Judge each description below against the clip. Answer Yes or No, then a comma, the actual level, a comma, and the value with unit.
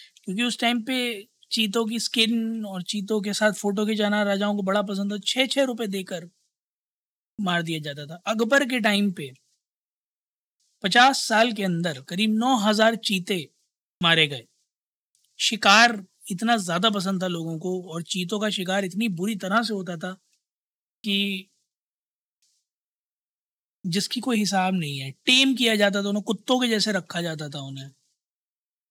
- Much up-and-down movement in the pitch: No, average, 3.6 semitones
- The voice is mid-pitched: No, high, 205 Hz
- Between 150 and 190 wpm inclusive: Yes, average, 155 wpm